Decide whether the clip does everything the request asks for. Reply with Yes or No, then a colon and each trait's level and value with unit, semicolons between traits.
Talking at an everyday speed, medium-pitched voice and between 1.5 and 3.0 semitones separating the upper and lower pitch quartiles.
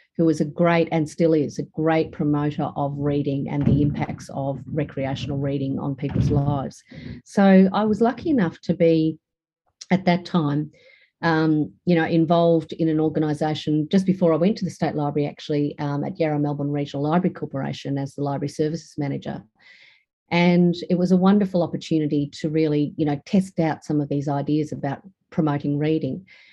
Yes: average, 175 wpm; medium, 155 Hz; narrow, 2.6 semitones